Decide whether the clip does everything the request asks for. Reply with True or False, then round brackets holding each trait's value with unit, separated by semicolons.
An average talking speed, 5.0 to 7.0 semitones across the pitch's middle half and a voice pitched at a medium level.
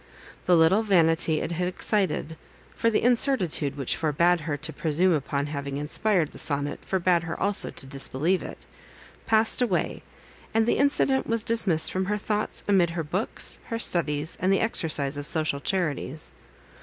True (165 wpm; 5.3 semitones; 170 Hz)